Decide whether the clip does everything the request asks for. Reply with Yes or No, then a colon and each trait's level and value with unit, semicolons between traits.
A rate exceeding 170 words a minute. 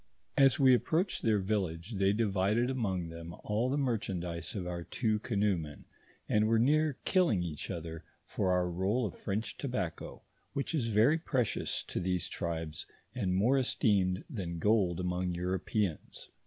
No: average, 155 wpm